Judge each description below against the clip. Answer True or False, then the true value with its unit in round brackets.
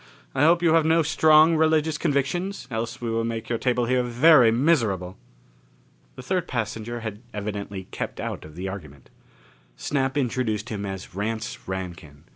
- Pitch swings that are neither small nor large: False (6.6 semitones)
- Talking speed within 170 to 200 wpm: False (160 wpm)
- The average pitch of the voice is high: False (120 Hz)